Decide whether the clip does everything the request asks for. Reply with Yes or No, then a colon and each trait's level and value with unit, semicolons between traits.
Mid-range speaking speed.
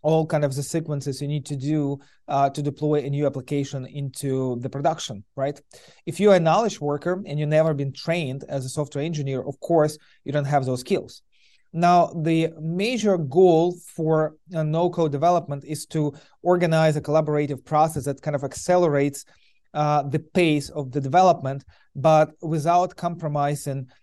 Yes: average, 165 wpm